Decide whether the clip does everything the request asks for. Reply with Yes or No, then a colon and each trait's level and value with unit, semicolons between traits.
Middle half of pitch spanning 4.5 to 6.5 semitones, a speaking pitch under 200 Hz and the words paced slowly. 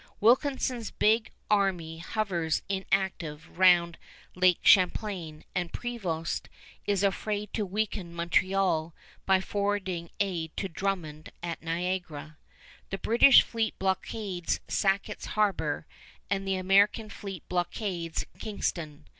No: average, 3.2 semitones; high, 190 Hz; slow, 105 wpm